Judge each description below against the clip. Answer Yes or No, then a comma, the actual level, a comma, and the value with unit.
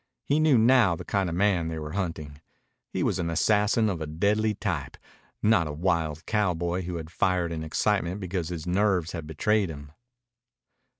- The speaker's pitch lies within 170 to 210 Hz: No, very low, 90 Hz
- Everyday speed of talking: Yes, average, 180 wpm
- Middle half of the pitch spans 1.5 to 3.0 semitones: No, average, 4.2 semitones